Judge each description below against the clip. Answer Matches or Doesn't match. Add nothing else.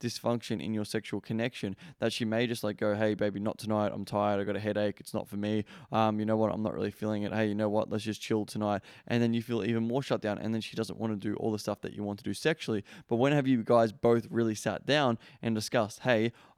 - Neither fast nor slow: Doesn't match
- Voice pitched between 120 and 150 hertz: Doesn't match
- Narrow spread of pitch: Matches